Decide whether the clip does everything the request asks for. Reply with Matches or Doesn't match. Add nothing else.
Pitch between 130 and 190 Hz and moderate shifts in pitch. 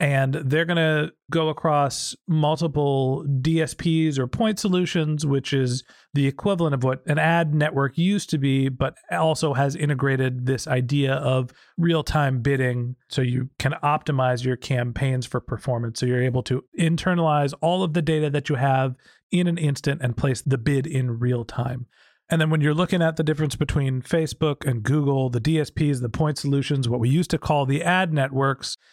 Matches